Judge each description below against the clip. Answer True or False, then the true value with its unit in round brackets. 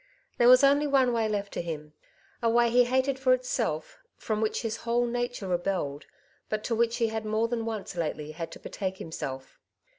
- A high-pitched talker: True (225 Hz)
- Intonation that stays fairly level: False (4.4 semitones)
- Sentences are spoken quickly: True (210 wpm)